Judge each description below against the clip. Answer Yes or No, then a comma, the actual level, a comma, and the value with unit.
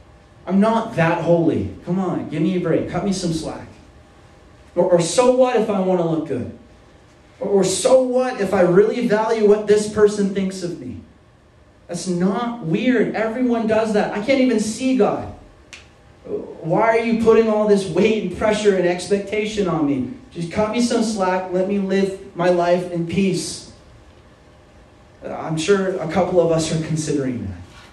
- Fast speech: No, average, 180 wpm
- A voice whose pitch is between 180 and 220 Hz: Yes, medium, 185 Hz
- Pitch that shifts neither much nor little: Yes, average, 4.4 semitones